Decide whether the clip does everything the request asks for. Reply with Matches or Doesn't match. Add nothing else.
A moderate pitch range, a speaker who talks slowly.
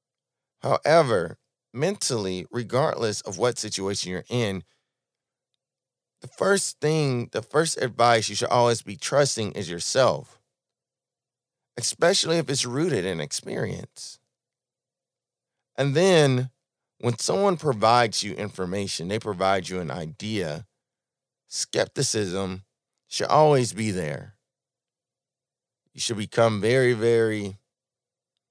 Matches